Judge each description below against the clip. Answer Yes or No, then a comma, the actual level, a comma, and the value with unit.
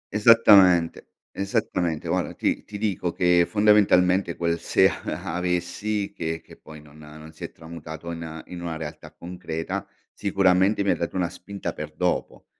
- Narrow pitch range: No, average, 3.3 semitones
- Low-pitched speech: Yes, very low, 90 Hz